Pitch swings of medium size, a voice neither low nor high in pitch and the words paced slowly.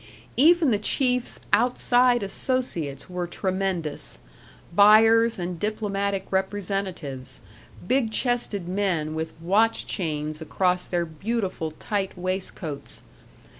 No: average, 4.6 semitones; high, 195 Hz; slow, 95 wpm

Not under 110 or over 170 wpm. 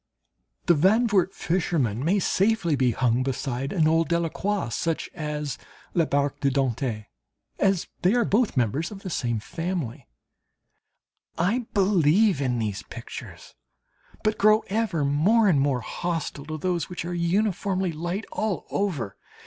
Yes: average, 140 wpm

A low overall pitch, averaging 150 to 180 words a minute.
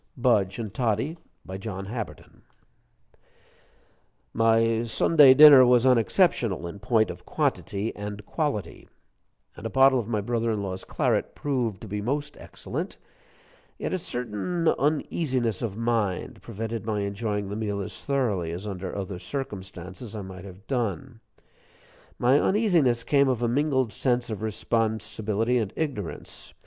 No: low, 115 Hz; average, 140 wpm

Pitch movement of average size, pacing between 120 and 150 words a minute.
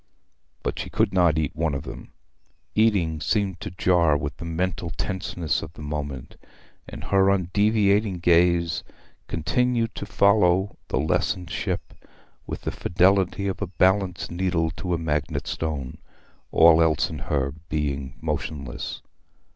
Yes: average, 3.7 semitones; average, 140 wpm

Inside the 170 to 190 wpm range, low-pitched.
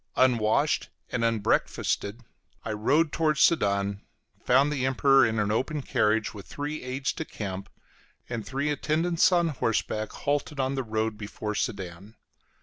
No: average, 145 wpm; low, 125 Hz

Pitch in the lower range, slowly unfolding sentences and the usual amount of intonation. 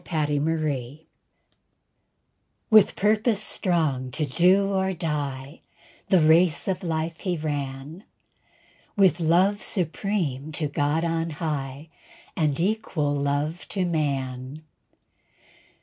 No: medium, 160 Hz; slow, 105 wpm; average, 4.0 semitones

